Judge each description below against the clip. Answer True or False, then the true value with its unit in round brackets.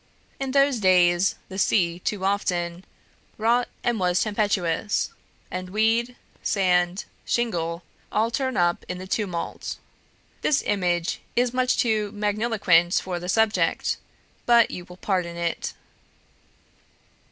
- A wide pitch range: False (4.1 semitones)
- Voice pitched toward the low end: False (195 Hz)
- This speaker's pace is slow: True (120 wpm)